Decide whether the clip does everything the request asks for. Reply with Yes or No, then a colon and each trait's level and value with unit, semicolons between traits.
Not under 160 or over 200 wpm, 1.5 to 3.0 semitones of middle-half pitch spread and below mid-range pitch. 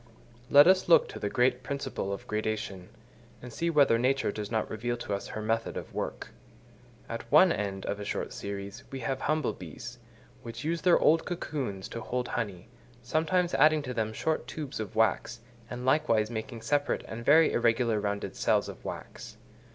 No: average, 180 wpm; average, 5.0 semitones; low, 120 Hz